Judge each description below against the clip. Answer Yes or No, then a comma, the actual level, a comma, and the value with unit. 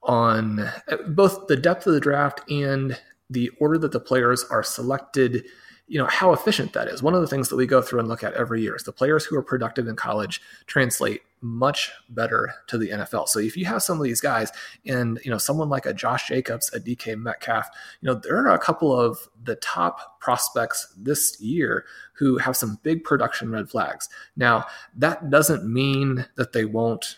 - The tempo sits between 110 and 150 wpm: No, fast, 205 wpm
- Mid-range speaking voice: No, low, 130 Hz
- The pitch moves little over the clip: No, average, 3.8 semitones